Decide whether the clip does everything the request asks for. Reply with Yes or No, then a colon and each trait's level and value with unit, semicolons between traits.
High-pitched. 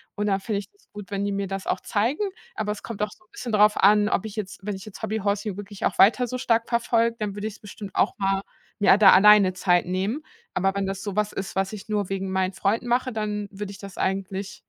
Yes: high, 205 Hz